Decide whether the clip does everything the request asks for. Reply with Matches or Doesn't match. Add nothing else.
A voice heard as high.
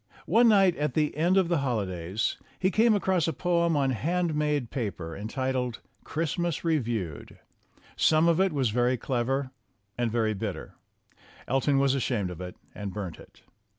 Doesn't match